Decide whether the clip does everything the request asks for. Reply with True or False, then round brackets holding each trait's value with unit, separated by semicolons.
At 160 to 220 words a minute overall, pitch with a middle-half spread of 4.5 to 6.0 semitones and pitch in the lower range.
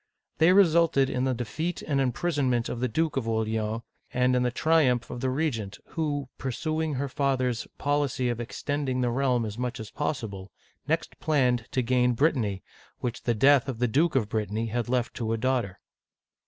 False (185 wpm; 3.6 semitones; 125 Hz)